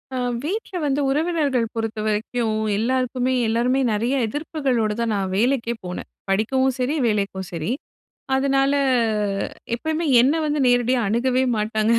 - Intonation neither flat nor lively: Yes, average, 3.8 semitones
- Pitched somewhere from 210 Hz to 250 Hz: Yes, high, 245 Hz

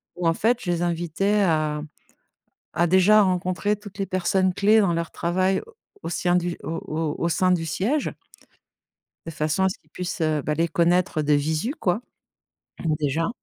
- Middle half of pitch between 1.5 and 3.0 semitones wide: Yes, average, 2.7 semitones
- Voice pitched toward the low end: No, medium, 175 Hz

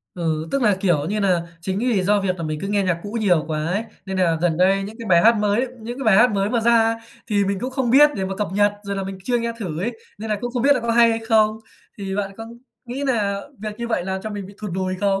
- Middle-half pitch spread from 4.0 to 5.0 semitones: No, average, 3.2 semitones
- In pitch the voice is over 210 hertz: No, high, 205 Hz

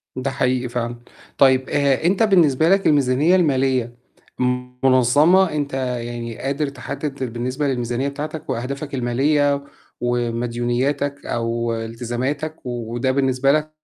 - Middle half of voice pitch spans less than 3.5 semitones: Yes, average, 3.1 semitones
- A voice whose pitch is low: Yes, low, 130 Hz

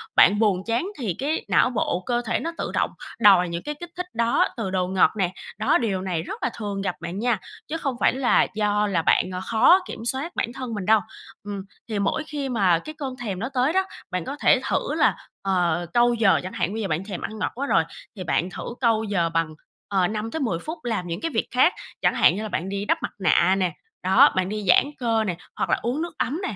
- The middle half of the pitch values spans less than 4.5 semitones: No, average, 5.0 semitones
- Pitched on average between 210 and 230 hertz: Yes, high, 215 Hz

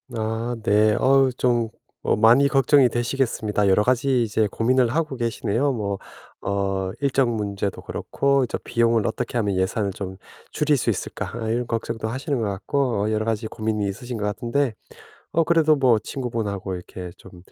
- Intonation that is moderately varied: Yes, average, 3.8 semitones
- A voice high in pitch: No, low, 115 Hz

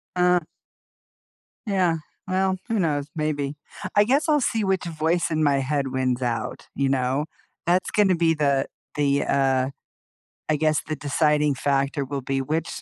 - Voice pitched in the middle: Yes, medium, 150 Hz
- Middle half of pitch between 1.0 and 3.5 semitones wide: No, average, 4.3 semitones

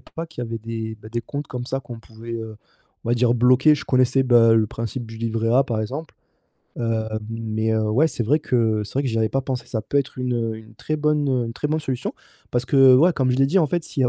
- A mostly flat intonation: No, average, 3.1 semitones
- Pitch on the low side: Yes, low, 120 Hz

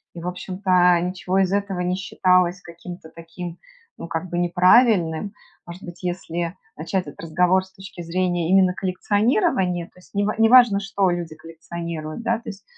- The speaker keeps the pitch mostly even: Yes, narrow, 2.0 semitones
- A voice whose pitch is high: No, medium, 180 Hz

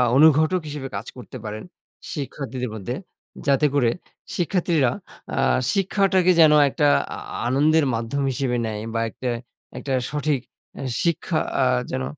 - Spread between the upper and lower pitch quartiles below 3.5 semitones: No, average, 4.3 semitones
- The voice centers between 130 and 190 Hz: Yes, medium, 140 Hz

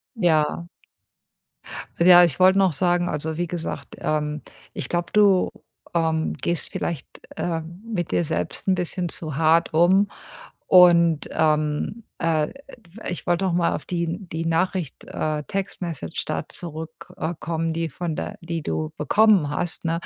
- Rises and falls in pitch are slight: Yes, narrow, 2.0 semitones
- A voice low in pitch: No, medium, 170 Hz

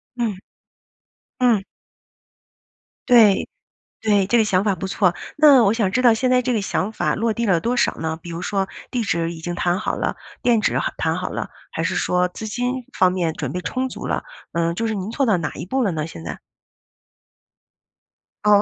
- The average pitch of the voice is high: Yes, high, 205 Hz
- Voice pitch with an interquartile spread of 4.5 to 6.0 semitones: Yes, average, 4.8 semitones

